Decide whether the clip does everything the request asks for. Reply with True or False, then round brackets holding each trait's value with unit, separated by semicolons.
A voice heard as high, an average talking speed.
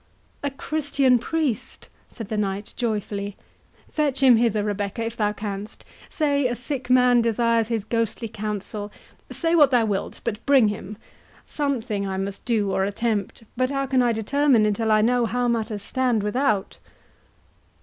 True (230 Hz; 150 wpm)